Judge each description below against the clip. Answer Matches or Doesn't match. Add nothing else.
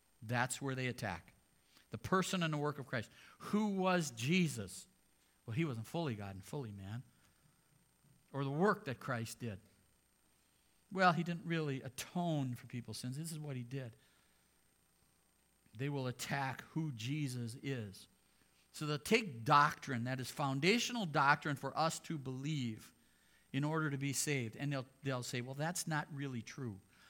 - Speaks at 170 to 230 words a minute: Doesn't match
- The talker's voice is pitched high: Doesn't match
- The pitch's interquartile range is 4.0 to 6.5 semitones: Matches